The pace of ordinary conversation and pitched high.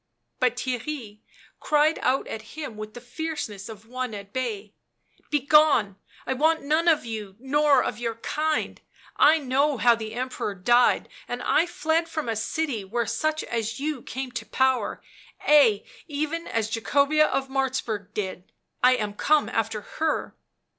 Yes: average, 160 wpm; very high, 255 Hz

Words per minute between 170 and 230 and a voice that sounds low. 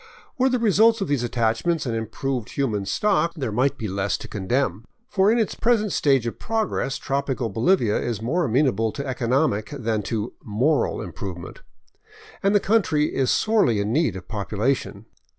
Yes: average, 180 wpm; low, 130 Hz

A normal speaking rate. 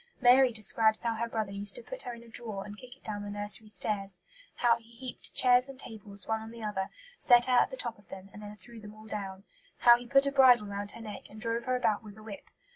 No: fast, 270 wpm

